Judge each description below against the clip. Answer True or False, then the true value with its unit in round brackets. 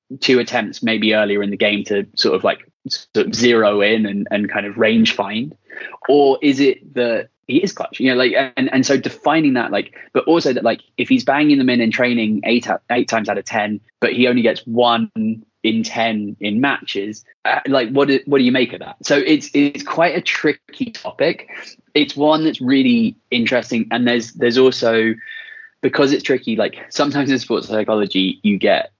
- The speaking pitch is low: True (125 Hz)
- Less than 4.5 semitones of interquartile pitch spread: False (5.1 semitones)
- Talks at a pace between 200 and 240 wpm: True (205 wpm)